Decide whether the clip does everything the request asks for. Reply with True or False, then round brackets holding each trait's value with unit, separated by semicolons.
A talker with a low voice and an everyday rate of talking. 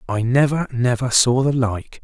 True (125 Hz; 175 wpm)